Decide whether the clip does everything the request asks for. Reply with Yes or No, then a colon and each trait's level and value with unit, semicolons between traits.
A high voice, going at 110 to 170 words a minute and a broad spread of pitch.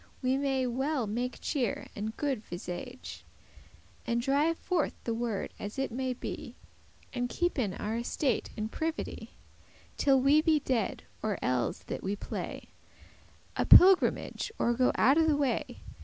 No: very high, 255 Hz; average, 150 wpm; average, 4.1 semitones